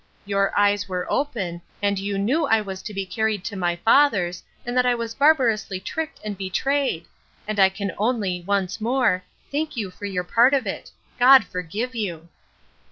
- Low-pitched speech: No, high, 205 Hz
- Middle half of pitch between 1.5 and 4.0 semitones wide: No, average, 4.6 semitones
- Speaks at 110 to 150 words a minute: No, average, 180 wpm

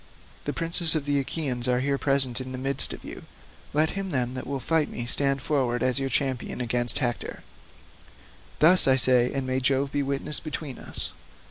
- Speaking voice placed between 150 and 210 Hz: No, low, 135 Hz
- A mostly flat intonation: Yes, narrow, 2.2 semitones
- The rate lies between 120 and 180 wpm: No, average, 195 wpm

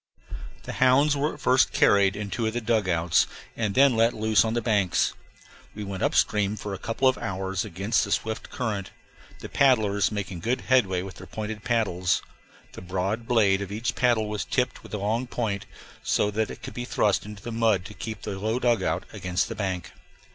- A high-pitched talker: No, low, 105 Hz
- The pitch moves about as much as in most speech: Yes, average, 3.1 semitones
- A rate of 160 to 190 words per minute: No, fast, 205 wpm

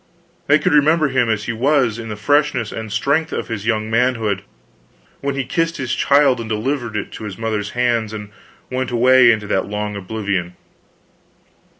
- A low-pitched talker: Yes, low, 115 Hz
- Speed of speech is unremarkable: Yes, average, 180 wpm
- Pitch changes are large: No, average, 3.8 semitones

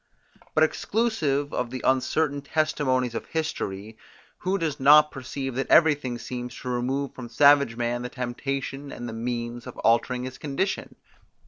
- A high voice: No, low, 130 Hz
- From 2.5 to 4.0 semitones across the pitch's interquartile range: Yes, average, 3.1 semitones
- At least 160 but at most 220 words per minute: No, average, 150 wpm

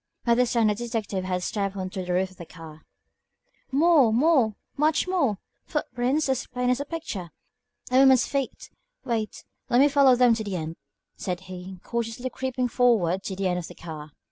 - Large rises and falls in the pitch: Yes, wide, 5.7 semitones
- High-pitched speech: Yes, high, 230 Hz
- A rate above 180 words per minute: Yes, average, 195 wpm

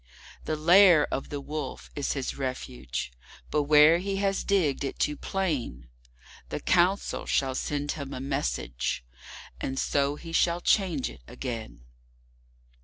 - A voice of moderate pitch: Yes, medium, 145 Hz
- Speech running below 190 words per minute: Yes, slow, 135 wpm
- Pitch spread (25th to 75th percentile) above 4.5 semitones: Yes, average, 4.9 semitones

